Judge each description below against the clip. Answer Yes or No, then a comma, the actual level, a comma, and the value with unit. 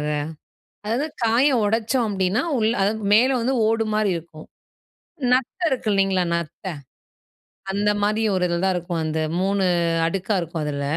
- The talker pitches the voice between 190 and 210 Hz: Yes, high, 200 Hz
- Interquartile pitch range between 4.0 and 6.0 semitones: Yes, average, 4.3 semitones